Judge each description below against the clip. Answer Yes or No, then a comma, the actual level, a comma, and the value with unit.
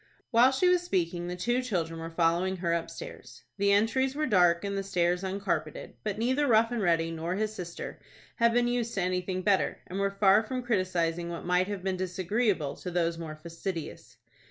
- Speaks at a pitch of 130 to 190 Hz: Yes, medium, 185 Hz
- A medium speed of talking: Yes, average, 195 wpm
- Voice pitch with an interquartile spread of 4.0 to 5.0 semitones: Yes, average, 4.3 semitones